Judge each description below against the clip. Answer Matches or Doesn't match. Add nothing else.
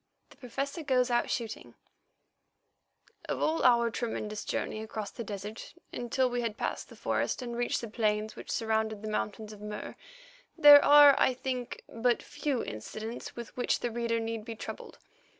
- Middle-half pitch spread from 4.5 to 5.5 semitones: Doesn't match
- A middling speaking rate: Matches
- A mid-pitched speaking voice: Doesn't match